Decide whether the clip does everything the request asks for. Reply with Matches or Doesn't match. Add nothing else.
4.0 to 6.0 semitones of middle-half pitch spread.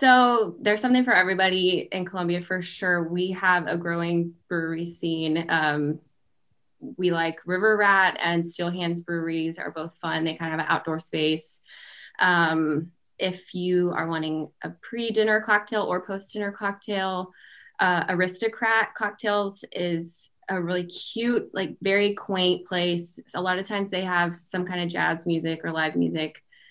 Doesn't match